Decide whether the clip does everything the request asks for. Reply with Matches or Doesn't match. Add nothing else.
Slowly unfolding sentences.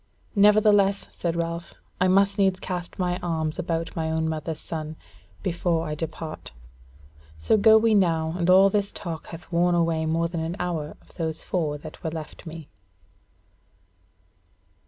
Doesn't match